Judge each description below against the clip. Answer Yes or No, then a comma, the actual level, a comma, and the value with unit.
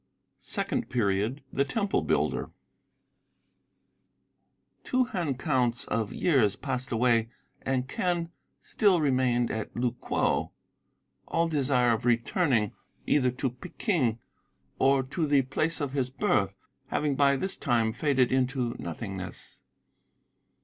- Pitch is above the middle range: No, low, 130 Hz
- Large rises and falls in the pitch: No, average, 3.5 semitones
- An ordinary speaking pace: No, slow, 115 wpm